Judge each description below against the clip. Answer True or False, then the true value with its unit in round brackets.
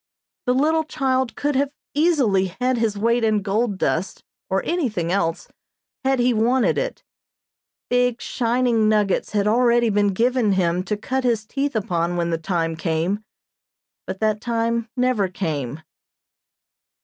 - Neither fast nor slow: True (145 wpm)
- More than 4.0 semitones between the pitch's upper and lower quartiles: True (4.6 semitones)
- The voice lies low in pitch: False (220 Hz)